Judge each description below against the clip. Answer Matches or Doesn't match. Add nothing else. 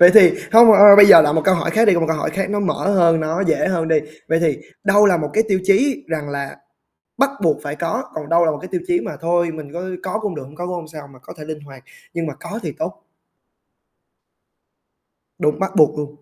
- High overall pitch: Doesn't match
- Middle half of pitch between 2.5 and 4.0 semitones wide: Doesn't match